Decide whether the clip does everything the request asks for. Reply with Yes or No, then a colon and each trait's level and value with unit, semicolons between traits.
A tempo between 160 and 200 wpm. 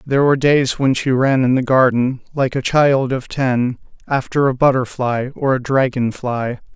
Yes: average, 185 wpm